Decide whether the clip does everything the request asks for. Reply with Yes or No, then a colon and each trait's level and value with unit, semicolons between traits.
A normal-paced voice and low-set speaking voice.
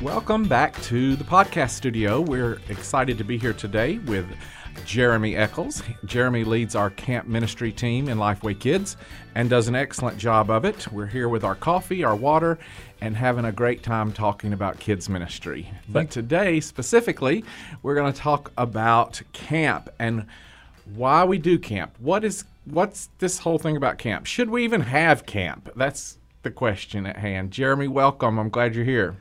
Yes: average, 175 wpm; low, 120 Hz